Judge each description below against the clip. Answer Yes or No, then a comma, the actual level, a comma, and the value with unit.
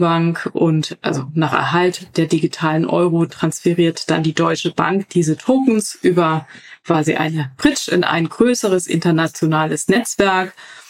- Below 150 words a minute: Yes, average, 130 wpm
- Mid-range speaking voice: Yes, medium, 165 Hz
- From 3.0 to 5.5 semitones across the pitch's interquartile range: No, narrow, 2.4 semitones